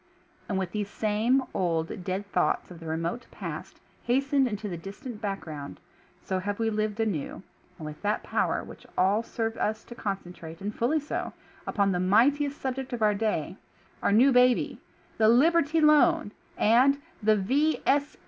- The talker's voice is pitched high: Yes, high, 215 Hz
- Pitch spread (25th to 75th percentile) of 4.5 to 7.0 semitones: Yes, average, 4.9 semitones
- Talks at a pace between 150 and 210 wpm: Yes, average, 165 wpm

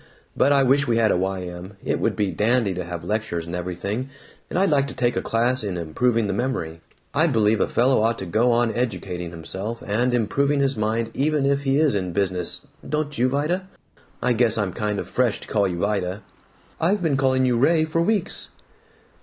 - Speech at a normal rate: No, fast, 210 wpm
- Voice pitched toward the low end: Yes, low, 115 Hz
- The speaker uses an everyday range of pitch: No, wide, 5.9 semitones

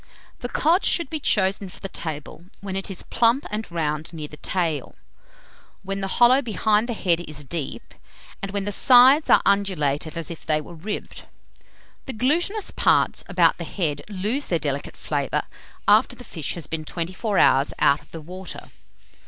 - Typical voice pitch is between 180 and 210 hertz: Yes, high, 190 Hz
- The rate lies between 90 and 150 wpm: No, average, 180 wpm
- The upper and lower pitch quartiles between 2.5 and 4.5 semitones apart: No, wide, 5.5 semitones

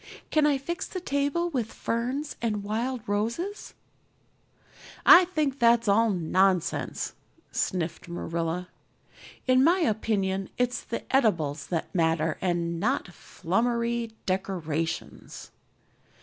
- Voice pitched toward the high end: Yes, high, 220 Hz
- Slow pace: Yes, slow, 105 wpm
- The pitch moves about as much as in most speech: No, wide, 6.8 semitones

